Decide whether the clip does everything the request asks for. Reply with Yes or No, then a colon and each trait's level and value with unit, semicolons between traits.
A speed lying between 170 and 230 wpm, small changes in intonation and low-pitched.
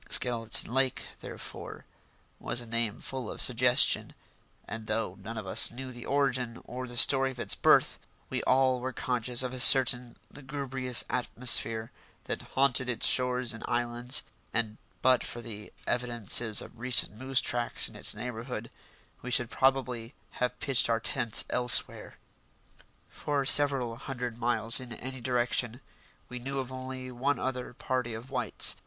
No: average, 155 wpm; narrow, 1.8 semitones; low, 125 Hz